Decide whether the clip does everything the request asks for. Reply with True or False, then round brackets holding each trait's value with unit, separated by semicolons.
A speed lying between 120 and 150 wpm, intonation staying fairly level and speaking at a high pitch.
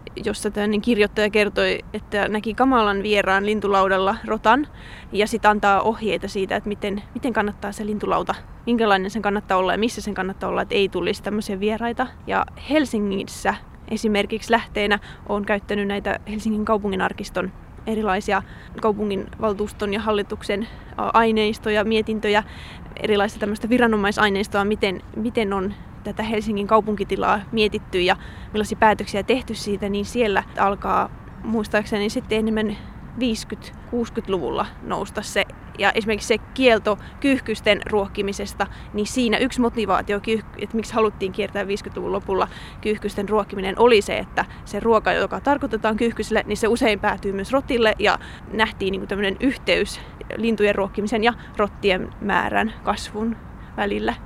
True (130 wpm; 1.5 semitones; 210 Hz)